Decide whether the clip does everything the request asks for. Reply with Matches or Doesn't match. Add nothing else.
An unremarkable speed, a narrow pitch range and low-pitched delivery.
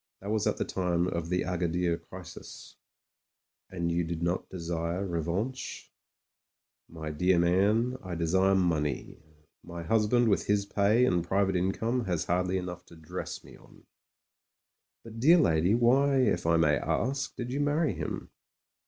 Doesn't match